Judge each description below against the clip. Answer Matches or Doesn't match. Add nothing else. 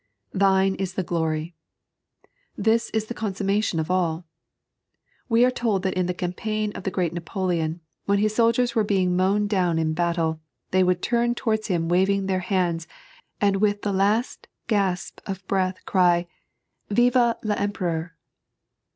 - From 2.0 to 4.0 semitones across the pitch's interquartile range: Matches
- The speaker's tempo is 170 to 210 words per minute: Doesn't match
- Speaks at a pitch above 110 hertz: Matches